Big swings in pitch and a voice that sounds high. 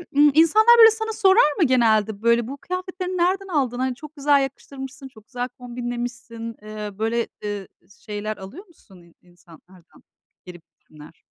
Yes: wide, 6.5 semitones; high, 245 Hz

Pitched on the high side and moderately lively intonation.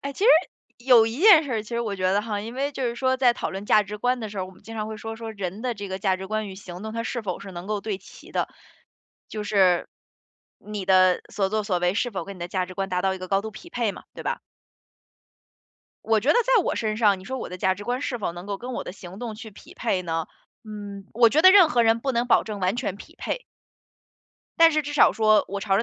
Yes: high, 215 Hz; average, 3.7 semitones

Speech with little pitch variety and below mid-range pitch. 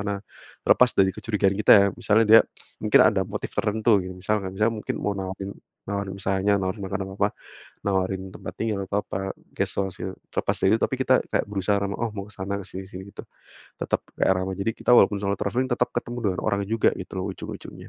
Yes: narrow, 2.1 semitones; low, 100 Hz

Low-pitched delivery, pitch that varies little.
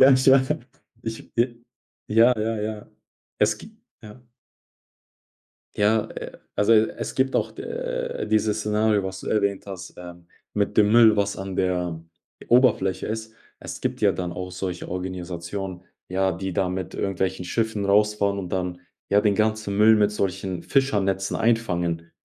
No: low, 105 Hz; average, 3.0 semitones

